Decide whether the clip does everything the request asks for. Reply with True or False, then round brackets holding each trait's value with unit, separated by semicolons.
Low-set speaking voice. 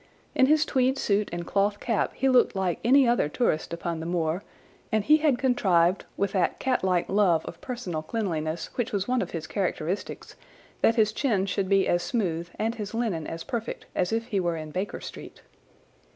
False (200 Hz)